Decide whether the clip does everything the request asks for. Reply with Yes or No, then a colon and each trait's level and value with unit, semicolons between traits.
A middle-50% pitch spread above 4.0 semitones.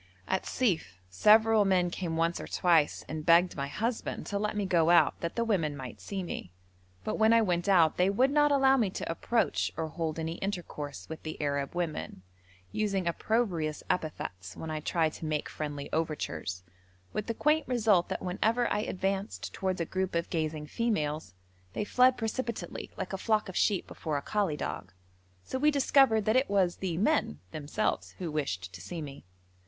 Yes: wide, 5.6 semitones